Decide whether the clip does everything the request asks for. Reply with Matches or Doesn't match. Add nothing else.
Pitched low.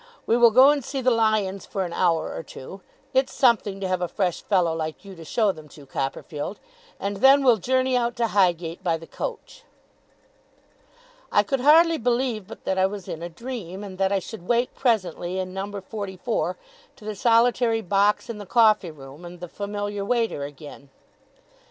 Doesn't match